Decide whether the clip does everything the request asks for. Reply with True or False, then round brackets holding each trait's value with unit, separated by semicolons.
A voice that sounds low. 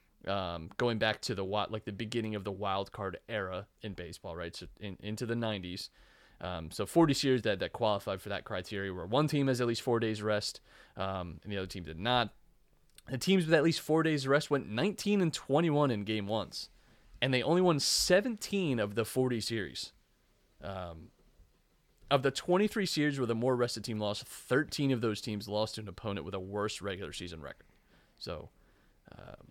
True (110 Hz)